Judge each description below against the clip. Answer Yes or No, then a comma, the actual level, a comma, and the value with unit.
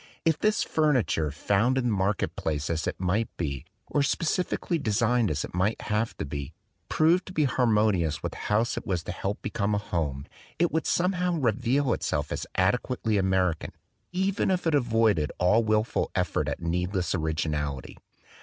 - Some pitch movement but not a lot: No, wide, 7.2 semitones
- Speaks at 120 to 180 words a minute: Yes, average, 175 wpm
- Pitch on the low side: Yes, low, 105 Hz